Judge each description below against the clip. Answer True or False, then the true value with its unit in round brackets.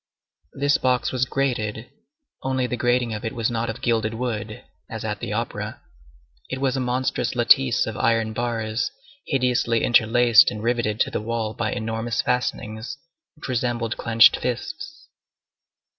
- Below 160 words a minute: True (150 wpm)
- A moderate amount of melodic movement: False (2.0 semitones)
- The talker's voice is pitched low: True (120 Hz)